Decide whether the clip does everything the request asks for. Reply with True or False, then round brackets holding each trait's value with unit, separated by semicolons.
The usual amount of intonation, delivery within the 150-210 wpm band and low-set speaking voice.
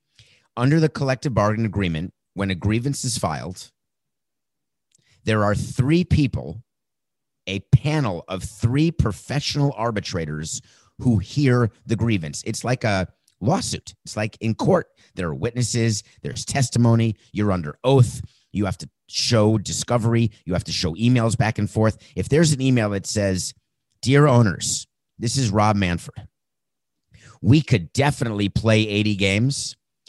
False (3.8 semitones; 140 wpm; 115 Hz)